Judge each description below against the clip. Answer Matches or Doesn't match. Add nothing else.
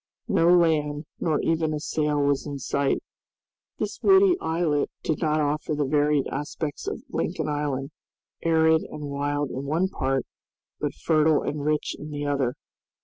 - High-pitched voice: Doesn't match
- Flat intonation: Matches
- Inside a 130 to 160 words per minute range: Matches